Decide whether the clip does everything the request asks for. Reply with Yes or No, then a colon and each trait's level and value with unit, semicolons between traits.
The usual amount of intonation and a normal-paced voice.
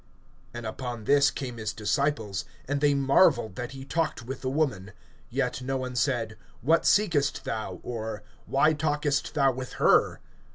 Yes: average, 3.9 semitones; average, 160 wpm